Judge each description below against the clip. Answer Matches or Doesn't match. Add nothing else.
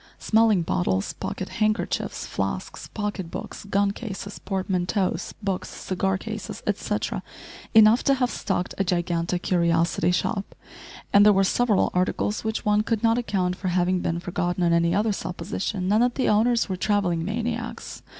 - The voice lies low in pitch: Doesn't match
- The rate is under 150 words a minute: Doesn't match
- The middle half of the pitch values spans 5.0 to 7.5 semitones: Doesn't match